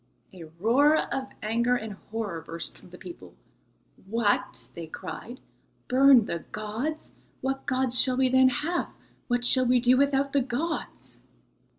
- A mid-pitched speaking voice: No, very high, 250 Hz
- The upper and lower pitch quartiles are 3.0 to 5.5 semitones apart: Yes, average, 3.9 semitones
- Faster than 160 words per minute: No, average, 150 wpm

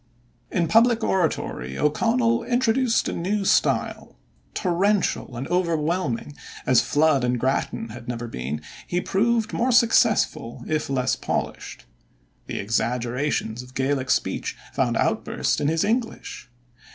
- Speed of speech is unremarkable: No, slow, 125 wpm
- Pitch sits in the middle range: Yes, medium, 155 Hz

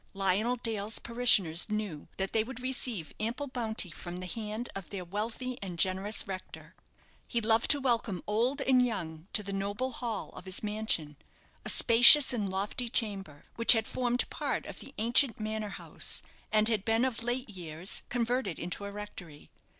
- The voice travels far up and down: No, average, 3.7 semitones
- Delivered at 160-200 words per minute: Yes, average, 175 wpm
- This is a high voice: Yes, high, 215 Hz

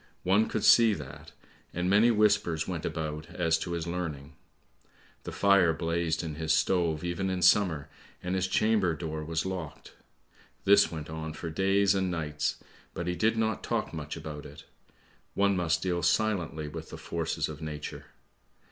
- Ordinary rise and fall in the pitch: Yes, average, 3.4 semitones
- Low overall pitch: Yes, very low, 85 Hz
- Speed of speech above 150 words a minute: Yes, average, 165 wpm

